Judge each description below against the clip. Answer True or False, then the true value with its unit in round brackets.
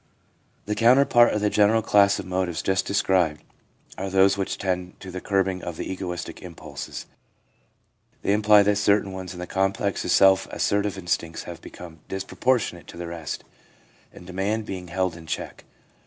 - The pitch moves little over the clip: True (2.3 semitones)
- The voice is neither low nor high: False (95 Hz)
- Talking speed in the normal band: True (170 wpm)